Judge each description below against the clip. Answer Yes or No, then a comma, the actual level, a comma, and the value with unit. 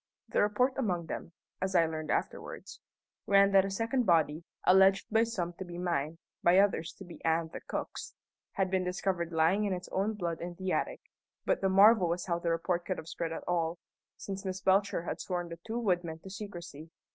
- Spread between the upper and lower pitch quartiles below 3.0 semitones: Yes, narrow, 2.6 semitones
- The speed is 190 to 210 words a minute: Yes, fast, 205 wpm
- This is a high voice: No, medium, 180 Hz